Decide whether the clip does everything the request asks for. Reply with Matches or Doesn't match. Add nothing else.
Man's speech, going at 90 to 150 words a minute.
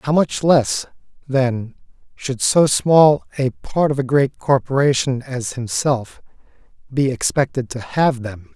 Matches